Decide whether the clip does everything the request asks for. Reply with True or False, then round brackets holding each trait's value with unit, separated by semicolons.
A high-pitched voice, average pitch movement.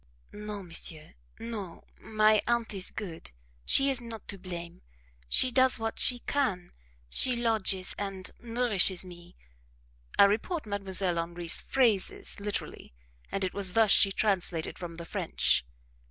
True (200 Hz; 4.1 semitones)